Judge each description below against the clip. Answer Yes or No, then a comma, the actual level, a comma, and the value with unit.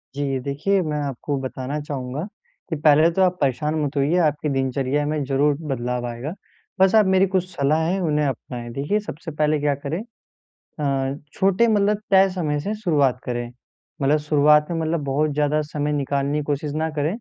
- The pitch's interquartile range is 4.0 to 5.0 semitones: No, average, 2.9 semitones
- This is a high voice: No, medium, 150 Hz